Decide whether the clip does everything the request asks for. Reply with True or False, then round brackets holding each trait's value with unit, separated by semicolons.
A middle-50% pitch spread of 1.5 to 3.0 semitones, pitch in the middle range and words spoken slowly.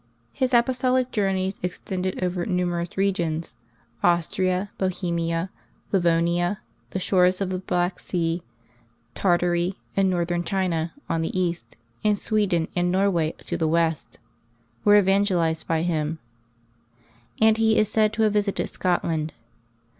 True (2.5 semitones; 180 Hz; 125 wpm)